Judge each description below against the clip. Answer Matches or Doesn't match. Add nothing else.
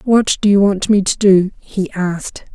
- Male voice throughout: Doesn't match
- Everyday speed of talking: Doesn't match